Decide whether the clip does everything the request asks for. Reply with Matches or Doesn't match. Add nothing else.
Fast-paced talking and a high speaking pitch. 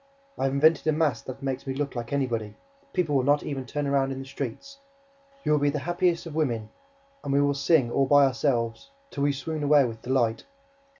Doesn't match